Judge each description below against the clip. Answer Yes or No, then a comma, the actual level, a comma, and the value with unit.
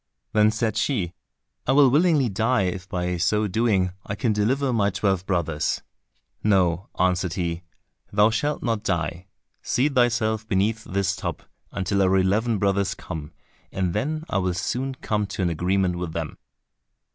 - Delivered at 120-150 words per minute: No, average, 160 wpm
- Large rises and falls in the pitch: No, average, 3.7 semitones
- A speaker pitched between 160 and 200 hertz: No, low, 100 Hz